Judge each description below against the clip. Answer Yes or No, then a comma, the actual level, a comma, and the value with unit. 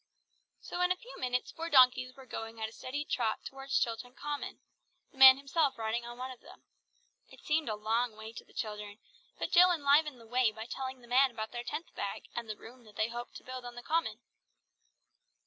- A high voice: Yes, very high, 250 Hz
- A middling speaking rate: No, fast, 215 wpm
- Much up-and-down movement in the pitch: No, average, 3.4 semitones